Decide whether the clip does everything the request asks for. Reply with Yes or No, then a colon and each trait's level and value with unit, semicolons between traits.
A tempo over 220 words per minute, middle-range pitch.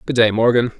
No: fast, 230 wpm; low, 115 Hz